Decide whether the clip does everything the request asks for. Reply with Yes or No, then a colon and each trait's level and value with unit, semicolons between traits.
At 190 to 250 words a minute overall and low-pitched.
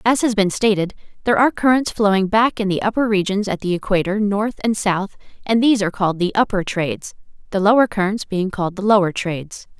No: average, 200 wpm; high, 200 Hz